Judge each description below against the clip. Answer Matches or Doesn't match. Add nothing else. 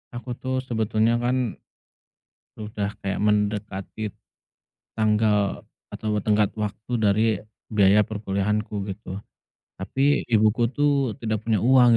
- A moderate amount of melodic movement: Doesn't match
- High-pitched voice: Doesn't match